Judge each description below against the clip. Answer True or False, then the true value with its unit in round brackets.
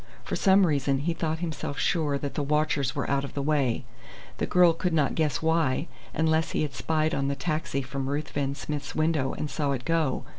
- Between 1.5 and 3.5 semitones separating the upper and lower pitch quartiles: True (2.5 semitones)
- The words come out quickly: True (210 wpm)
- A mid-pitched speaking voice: True (150 Hz)